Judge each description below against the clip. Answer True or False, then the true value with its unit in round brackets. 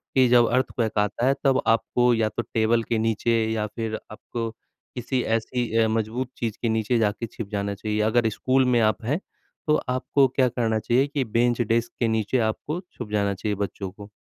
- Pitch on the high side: False (115 Hz)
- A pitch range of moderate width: False (2.1 semitones)